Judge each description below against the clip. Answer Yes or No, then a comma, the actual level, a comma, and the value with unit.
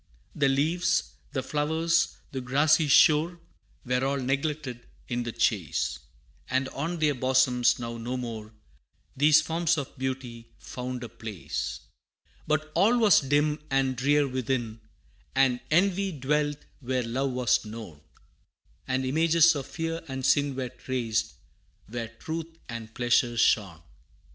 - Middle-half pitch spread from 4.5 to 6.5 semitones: No, average, 4.0 semitones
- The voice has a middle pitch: No, low, 130 Hz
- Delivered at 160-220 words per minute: No, slow, 135 wpm